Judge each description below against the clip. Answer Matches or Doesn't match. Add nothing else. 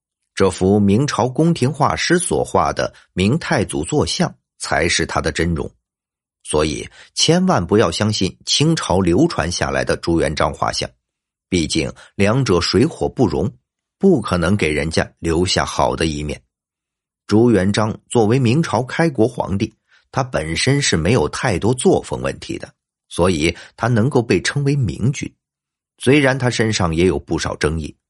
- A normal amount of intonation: Doesn't match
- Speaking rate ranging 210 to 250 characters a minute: Matches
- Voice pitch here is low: Matches